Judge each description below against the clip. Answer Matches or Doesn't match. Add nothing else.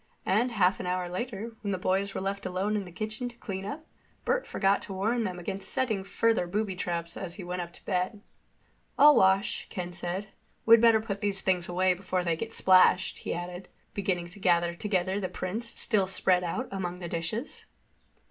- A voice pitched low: Doesn't match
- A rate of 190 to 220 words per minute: Matches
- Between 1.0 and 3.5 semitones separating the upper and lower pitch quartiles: Matches